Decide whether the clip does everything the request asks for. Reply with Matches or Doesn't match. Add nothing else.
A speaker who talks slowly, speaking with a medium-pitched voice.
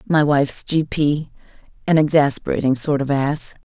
Matches